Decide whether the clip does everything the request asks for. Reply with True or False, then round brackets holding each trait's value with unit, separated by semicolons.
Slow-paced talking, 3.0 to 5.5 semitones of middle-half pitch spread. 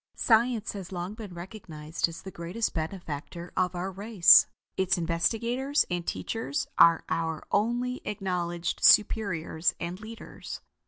True (125 wpm; 4.3 semitones)